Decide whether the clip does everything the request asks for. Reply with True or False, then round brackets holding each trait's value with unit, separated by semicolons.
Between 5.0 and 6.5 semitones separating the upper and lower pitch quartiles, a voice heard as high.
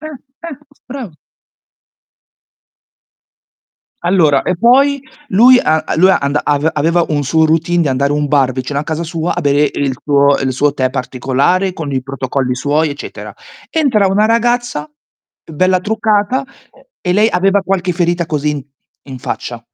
False (5.6 semitones; 160 Hz)